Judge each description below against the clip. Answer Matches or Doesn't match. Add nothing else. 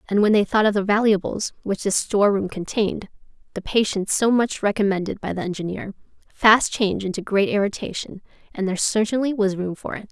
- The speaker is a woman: Matches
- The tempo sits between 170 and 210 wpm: Matches